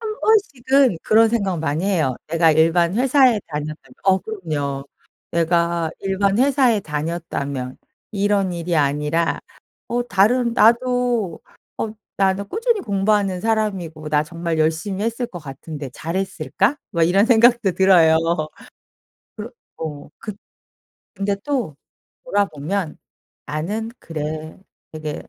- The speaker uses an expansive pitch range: Yes, wide, 5.7 semitones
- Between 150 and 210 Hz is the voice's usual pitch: Yes, high, 190 Hz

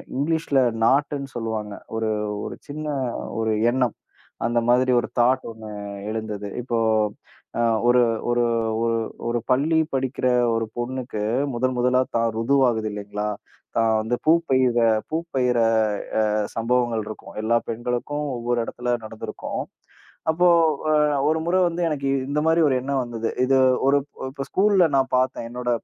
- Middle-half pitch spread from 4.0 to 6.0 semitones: No, average, 3.3 semitones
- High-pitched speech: No, low, 125 Hz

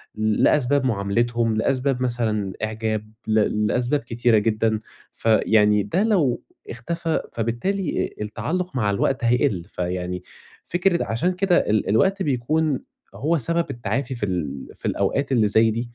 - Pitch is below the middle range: Yes, low, 115 Hz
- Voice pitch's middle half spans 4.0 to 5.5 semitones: Yes, average, 4.9 semitones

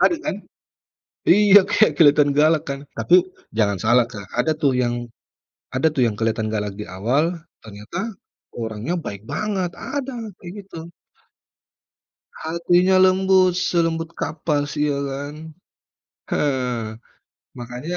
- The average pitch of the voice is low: No, medium, 145 Hz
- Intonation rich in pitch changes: Yes, wide, 6.7 semitones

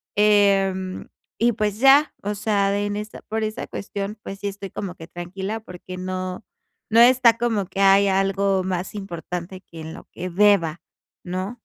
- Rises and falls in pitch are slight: Yes, narrow, 2.2 semitones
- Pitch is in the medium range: No, high, 195 Hz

